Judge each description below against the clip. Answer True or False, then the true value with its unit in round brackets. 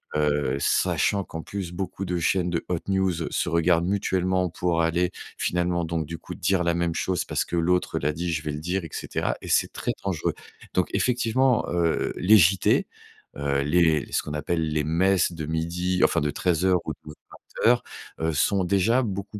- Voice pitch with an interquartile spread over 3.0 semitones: False (2.5 semitones)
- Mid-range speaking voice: False (85 Hz)